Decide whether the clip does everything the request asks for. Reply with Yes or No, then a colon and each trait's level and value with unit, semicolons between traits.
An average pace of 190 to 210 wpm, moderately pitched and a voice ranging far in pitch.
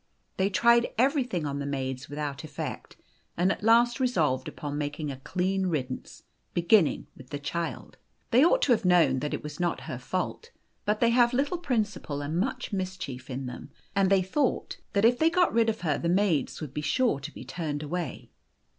Yes: average, 195 wpm; medium, 180 Hz; wide, 8.0 semitones